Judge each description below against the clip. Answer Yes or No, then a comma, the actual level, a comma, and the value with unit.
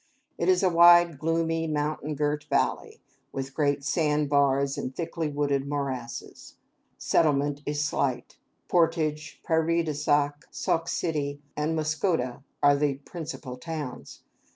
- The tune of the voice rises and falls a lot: No, narrow, 2.4 semitones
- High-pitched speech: No, medium, 150 Hz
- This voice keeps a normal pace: No, slow, 130 wpm